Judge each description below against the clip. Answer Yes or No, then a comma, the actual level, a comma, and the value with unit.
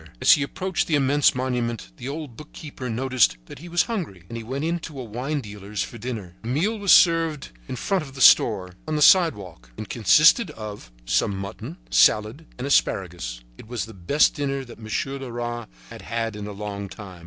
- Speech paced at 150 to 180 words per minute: No, average, 200 wpm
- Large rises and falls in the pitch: Yes, wide, 6.1 semitones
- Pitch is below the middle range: Yes, low, 125 Hz